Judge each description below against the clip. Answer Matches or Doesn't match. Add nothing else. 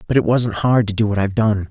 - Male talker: Matches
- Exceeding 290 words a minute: Matches